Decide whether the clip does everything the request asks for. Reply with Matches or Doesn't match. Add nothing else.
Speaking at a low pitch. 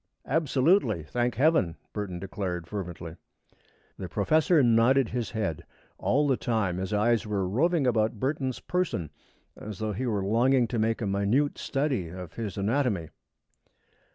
Matches